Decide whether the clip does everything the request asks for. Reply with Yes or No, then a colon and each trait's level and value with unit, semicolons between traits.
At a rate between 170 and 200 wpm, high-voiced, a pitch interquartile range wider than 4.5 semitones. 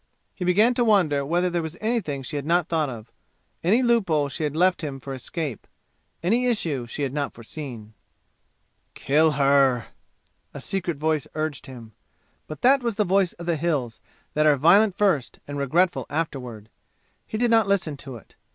No: average, 180 wpm; medium, 155 Hz; average, 5.1 semitones